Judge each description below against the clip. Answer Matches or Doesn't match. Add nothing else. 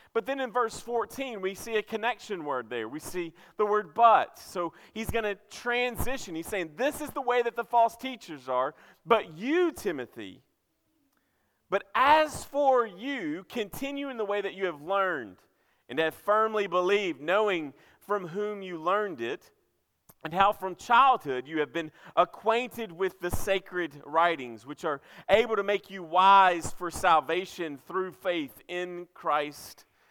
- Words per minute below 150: Doesn't match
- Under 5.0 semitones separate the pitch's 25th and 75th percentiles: Doesn't match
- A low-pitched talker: Doesn't match